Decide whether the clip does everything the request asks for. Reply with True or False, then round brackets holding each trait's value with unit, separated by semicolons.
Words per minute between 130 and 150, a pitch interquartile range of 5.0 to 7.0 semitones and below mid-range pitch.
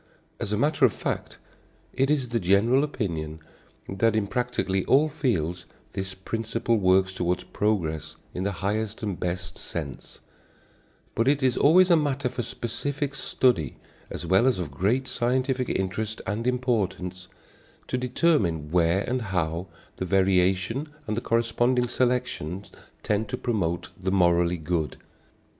True (145 wpm; 5.5 semitones; 105 Hz)